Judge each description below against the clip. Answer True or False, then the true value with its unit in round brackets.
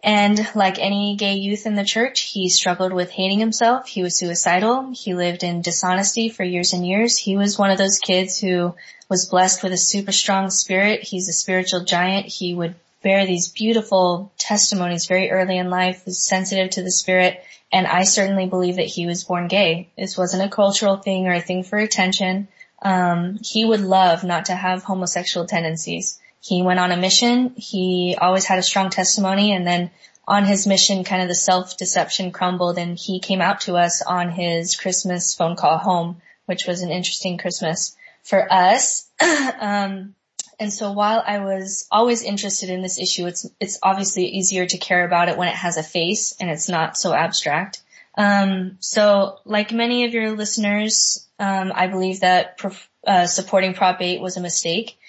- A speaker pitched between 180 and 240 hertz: True (185 Hz)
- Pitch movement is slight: True (1.9 semitones)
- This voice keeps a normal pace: True (190 wpm)